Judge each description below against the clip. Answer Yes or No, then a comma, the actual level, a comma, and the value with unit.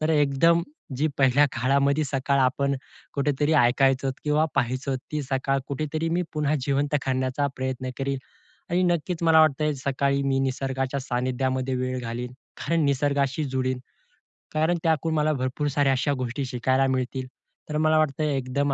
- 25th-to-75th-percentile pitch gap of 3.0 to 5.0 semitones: No, narrow, 2.6 semitones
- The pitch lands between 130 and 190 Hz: Yes, medium, 140 Hz